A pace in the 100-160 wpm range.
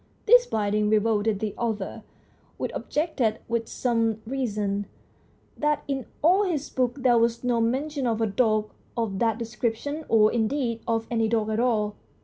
Yes: average, 155 wpm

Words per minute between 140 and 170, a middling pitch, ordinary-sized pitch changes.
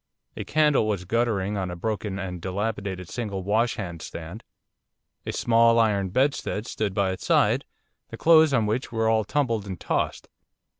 No: average, 160 wpm; low, 105 Hz; average, 3.5 semitones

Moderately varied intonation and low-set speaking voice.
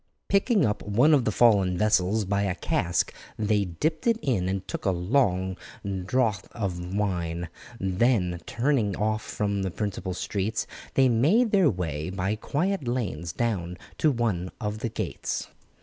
Yes: average, 4.6 semitones; low, 105 Hz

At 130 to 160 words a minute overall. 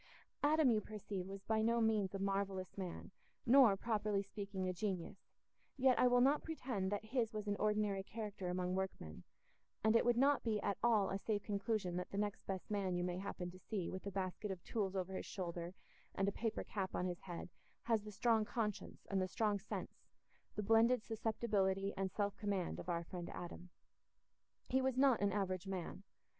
No: average, 200 wpm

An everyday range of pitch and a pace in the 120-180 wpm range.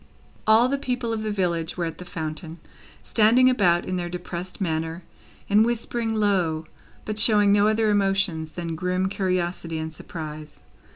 Yes: average, 4.5 semitones; average, 160 wpm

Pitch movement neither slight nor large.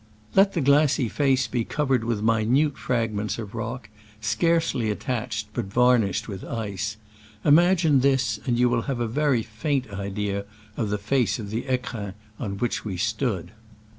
Yes: average, 3.9 semitones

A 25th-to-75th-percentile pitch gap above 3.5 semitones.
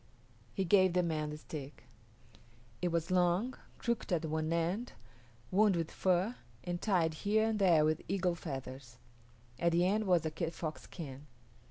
No: average, 3.2 semitones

